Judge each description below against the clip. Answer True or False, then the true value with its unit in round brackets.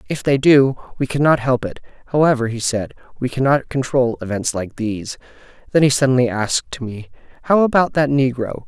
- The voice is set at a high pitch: False (130 Hz)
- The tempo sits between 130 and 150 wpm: False (175 wpm)